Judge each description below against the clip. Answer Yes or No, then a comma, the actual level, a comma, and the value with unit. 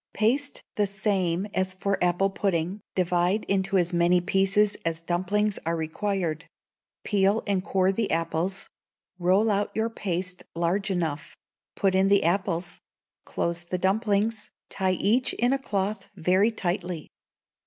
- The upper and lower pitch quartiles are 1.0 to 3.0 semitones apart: Yes, narrow, 2.6 semitones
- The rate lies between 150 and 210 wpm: No, average, 140 wpm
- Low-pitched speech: No, high, 190 Hz